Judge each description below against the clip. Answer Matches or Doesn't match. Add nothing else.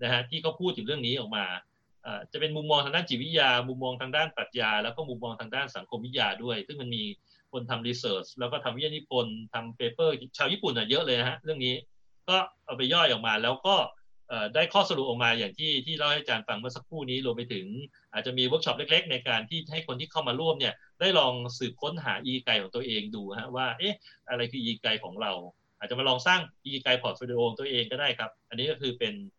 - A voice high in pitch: Doesn't match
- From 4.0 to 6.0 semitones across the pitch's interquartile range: Matches